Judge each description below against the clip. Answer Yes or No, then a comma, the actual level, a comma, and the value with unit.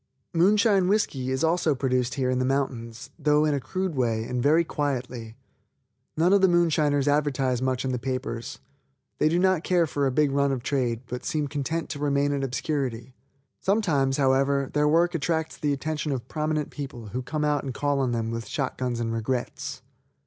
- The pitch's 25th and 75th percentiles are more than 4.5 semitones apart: No, average, 3.3 semitones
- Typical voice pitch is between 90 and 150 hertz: Yes, medium, 140 Hz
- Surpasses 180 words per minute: Yes, average, 190 wpm